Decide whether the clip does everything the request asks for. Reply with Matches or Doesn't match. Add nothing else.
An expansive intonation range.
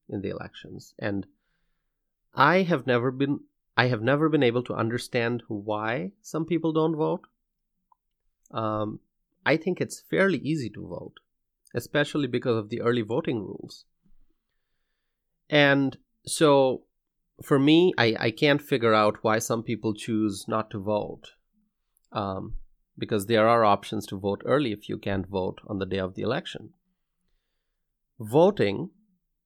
Matches